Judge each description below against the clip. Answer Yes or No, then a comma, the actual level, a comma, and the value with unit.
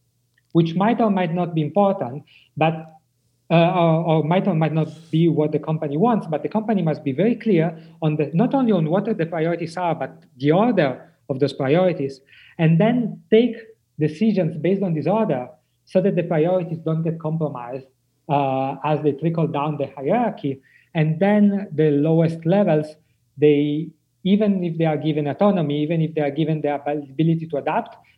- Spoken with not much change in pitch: No, average, 3.8 semitones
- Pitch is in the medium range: Yes, medium, 160 Hz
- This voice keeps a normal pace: Yes, average, 180 wpm